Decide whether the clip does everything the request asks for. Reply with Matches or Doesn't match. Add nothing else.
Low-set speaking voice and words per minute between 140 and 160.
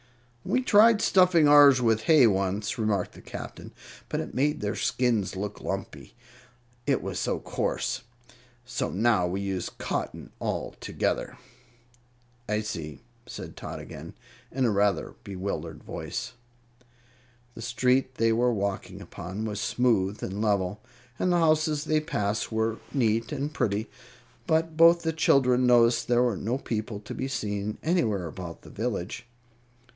Matches